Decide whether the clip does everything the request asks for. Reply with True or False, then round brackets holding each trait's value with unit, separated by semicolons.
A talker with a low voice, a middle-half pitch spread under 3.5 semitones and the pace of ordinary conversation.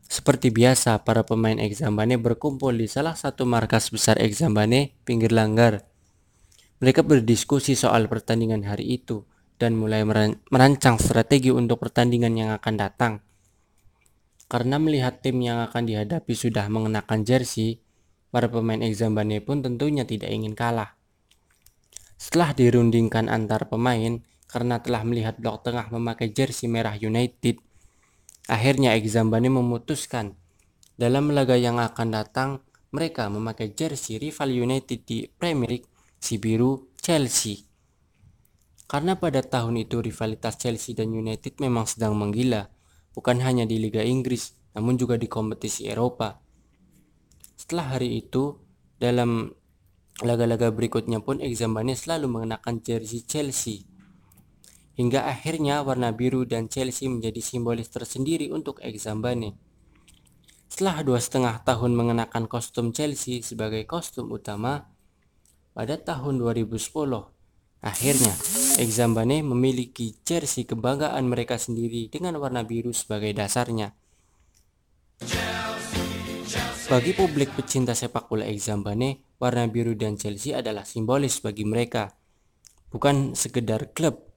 True (115 Hz; 2.9 semitones; 115 wpm)